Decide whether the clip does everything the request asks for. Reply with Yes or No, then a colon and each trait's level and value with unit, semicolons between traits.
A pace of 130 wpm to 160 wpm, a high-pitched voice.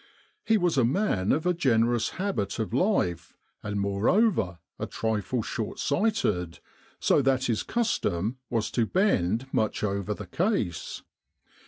No: average, 140 wpm; low, 115 Hz